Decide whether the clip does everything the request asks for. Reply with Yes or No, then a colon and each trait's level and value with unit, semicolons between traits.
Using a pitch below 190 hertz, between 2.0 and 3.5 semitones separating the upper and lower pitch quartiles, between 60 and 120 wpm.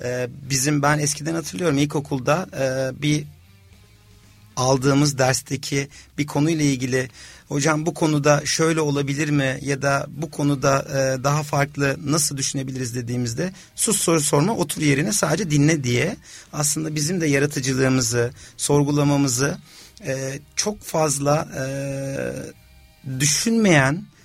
Yes: medium, 140 Hz; narrow, 2.4 semitones; average, 105 wpm